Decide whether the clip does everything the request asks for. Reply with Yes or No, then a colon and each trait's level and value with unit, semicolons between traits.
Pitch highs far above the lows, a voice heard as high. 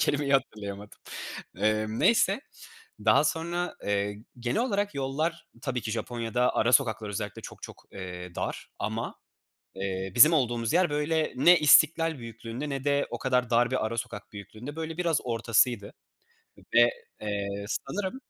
No: wide, 6.0 semitones; low, 120 Hz